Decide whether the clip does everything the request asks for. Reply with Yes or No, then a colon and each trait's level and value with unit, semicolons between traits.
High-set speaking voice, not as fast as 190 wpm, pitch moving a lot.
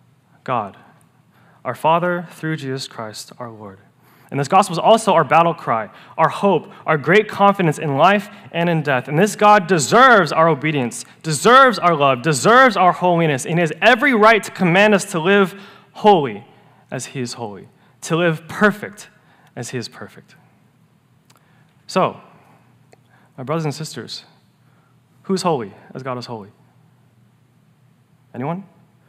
No: medium, 160 Hz; average, 145 wpm; wide, 6.0 semitones